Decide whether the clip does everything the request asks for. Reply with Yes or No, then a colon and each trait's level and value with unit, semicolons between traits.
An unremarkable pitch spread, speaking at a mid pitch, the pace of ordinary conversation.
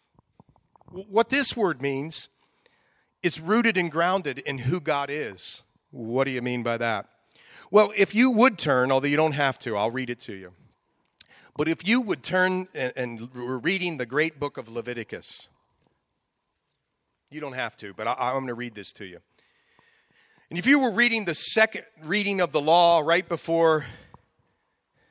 No: wide, 7.3 semitones; medium, 160 Hz; average, 175 wpm